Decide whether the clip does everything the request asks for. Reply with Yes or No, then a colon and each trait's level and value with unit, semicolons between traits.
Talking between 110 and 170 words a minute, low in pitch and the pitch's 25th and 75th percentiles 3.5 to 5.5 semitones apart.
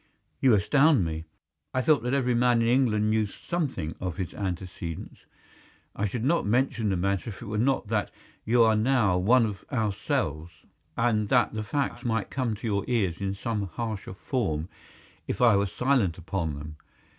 No: average, 180 wpm; low, 105 Hz; average, 4.2 semitones